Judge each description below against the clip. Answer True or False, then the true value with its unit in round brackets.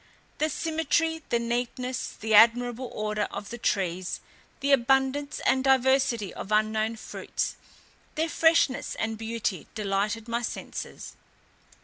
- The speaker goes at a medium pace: False (120 wpm)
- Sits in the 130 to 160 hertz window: False (235 Hz)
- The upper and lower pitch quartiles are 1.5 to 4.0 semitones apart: True (3.7 semitones)